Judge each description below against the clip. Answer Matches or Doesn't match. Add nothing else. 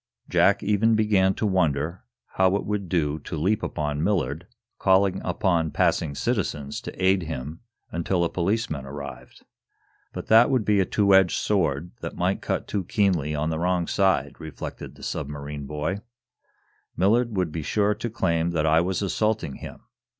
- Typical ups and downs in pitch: Matches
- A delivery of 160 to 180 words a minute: Matches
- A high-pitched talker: Doesn't match